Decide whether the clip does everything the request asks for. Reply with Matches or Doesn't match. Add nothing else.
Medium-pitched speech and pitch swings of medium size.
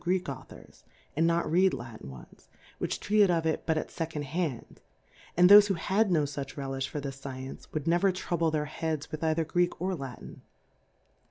Matches